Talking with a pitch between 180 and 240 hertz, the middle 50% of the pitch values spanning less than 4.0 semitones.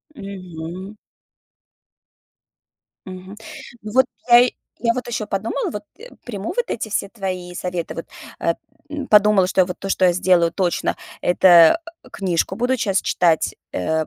Yes: high, 190 Hz; average, 3.3 semitones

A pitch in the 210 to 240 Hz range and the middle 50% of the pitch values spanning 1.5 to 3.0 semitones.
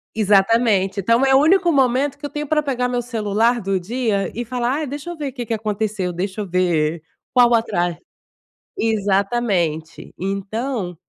No: high, 225 Hz; average, 4.6 semitones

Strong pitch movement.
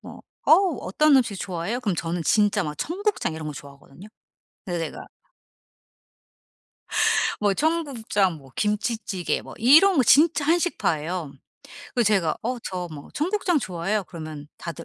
Yes: wide, 9.0 semitones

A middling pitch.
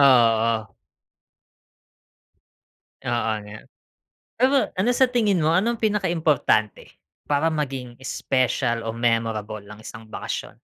No: low, 125 Hz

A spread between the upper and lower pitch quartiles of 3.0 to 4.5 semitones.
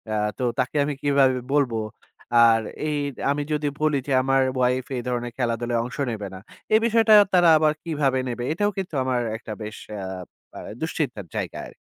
Yes: average, 4.1 semitones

